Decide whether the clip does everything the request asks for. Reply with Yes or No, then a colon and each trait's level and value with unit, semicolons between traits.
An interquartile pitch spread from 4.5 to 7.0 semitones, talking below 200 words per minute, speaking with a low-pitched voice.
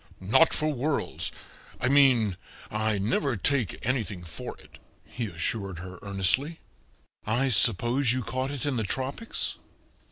Yes: average, 5.3 semitones; slow, 135 wpm; low, 120 Hz